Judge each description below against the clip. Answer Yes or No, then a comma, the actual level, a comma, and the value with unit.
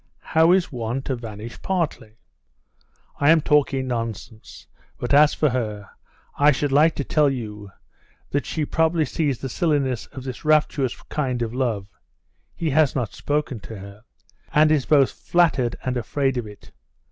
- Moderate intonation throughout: Yes, average, 4.4 semitones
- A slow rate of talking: No, average, 160 wpm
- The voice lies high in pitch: No, low, 135 Hz